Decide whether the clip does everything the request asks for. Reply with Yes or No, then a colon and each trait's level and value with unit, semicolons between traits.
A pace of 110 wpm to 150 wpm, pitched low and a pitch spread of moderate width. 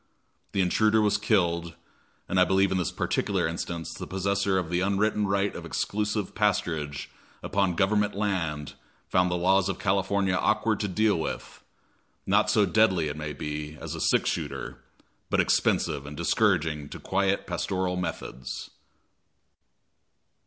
Yes: average, 145 wpm; very low, 95 Hz; average, 3.1 semitones